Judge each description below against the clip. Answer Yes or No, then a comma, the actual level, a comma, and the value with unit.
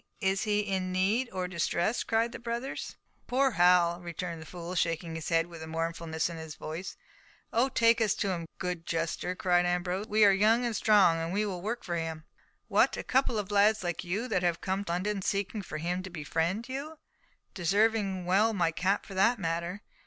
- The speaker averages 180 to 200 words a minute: Yes, average, 195 wpm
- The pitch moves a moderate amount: Yes, average, 3.8 semitones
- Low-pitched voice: No, medium, 185 Hz